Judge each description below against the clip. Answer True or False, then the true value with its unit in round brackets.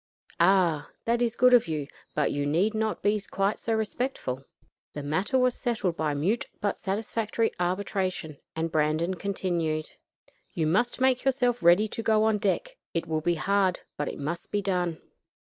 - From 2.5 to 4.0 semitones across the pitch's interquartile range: False (5.5 semitones)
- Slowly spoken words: False (170 wpm)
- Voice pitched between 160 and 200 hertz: True (190 Hz)